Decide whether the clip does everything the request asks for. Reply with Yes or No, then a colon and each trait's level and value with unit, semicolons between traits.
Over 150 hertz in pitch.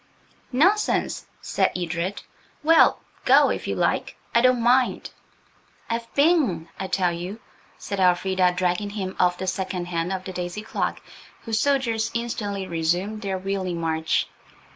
Yes: high, 190 Hz